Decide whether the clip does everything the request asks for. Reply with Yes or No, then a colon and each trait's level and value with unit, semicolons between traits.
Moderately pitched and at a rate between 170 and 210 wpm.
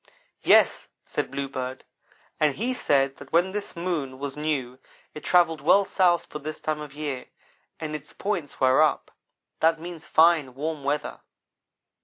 No: medium, 150 Hz; average, 155 wpm